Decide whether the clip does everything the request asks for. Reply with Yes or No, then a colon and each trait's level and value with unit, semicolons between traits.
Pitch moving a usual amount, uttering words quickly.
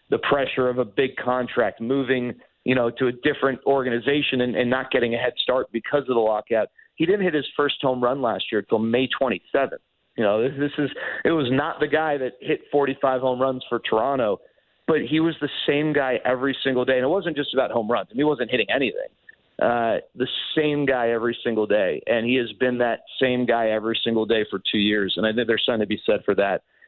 Yes: average, 3.4 semitones; fast, 240 wpm